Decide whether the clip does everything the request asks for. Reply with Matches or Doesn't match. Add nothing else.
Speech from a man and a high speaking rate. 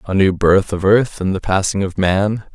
Matches